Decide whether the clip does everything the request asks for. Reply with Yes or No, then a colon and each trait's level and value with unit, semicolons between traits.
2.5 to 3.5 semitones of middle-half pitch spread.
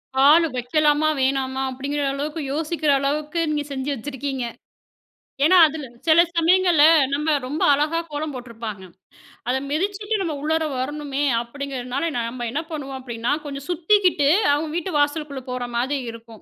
Yes: average, 3.1 semitones